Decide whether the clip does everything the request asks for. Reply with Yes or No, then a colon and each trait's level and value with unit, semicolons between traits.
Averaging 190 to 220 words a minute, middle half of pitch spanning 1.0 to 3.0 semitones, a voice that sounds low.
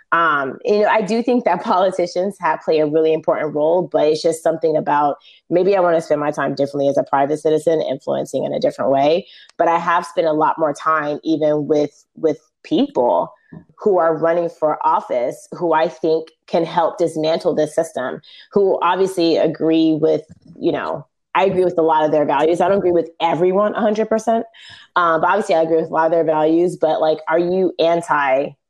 No: fast, 205 wpm; narrow, 2.4 semitones; medium, 165 Hz